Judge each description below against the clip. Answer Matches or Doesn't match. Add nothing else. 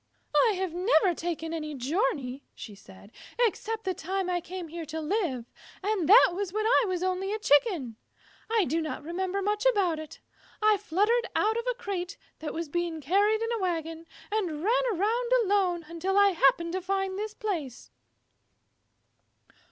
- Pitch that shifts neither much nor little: Matches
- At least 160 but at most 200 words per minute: Matches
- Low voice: Doesn't match